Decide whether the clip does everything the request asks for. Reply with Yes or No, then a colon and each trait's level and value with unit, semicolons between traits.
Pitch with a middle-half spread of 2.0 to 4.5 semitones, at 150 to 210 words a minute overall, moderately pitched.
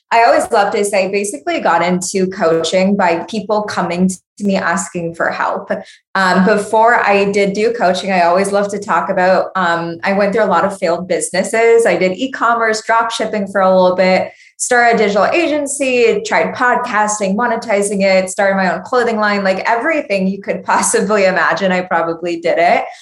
No: average, 3.3 semitones; average, 185 wpm; high, 200 Hz